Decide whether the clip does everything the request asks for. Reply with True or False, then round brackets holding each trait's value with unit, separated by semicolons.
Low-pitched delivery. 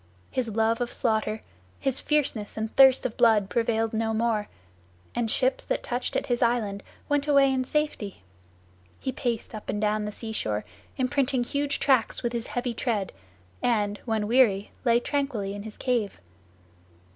False (235 Hz)